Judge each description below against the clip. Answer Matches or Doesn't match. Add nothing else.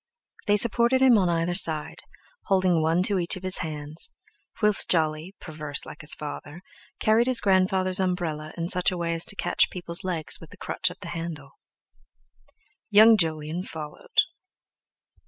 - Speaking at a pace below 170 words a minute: Matches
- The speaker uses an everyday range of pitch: Matches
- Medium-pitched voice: Matches